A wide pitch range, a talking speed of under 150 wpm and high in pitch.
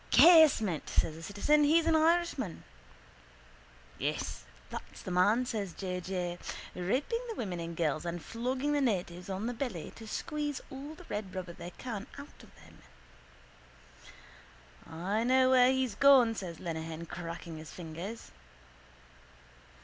Yes: wide, 7.3 semitones; average, 140 wpm; high, 210 Hz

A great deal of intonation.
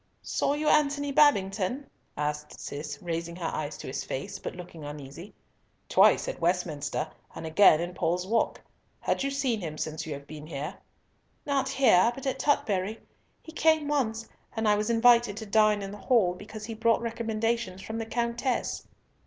Yes: wide, 6.0 semitones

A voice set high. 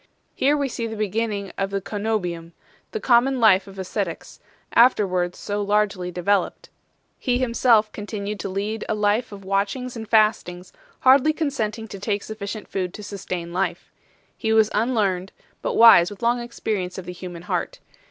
Yes: high, 210 Hz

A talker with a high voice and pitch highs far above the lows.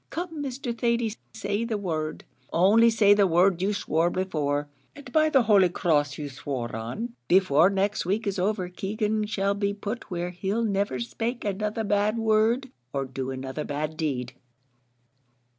Yes: high, 200 Hz; wide, 5.8 semitones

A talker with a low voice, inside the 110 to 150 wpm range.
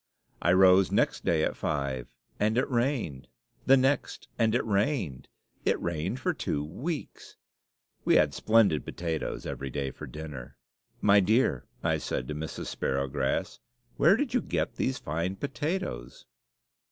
Yes: very low, 95 Hz; average, 145 wpm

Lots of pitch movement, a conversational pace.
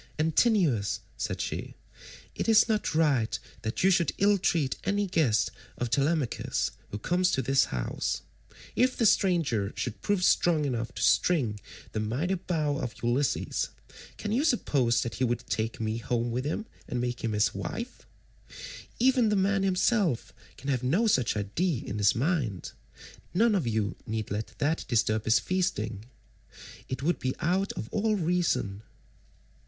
Yes: wide, 8.6 semitones; average, 160 wpm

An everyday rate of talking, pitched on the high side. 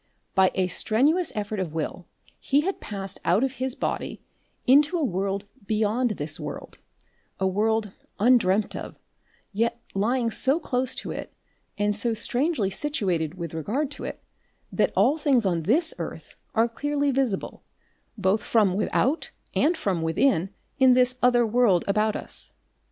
Yes: average, 150 wpm; high, 220 Hz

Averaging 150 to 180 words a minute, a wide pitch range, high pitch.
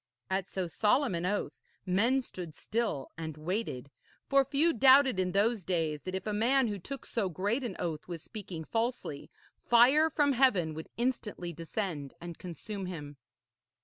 Yes: average, 165 wpm; wide, 6.1 semitones; high, 195 Hz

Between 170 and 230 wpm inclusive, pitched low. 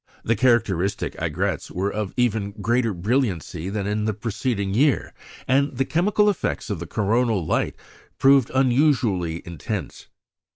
No: slow, 135 wpm; low, 110 Hz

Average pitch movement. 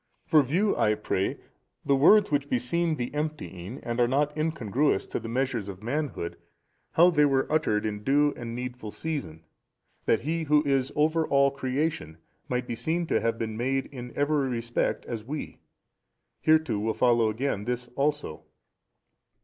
Yes: average, 4.6 semitones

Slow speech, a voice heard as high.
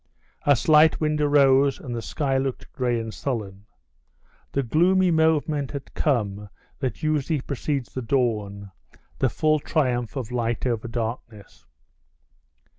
No: slow, 130 wpm; low, 130 Hz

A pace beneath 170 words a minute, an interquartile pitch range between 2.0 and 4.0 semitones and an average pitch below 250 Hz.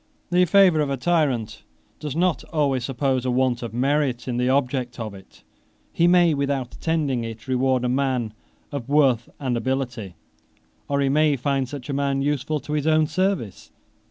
No: average, 180 wpm; average, 3.3 semitones; low, 135 Hz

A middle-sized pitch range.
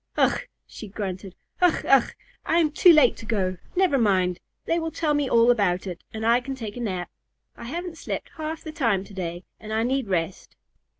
No: wide, 7.9 semitones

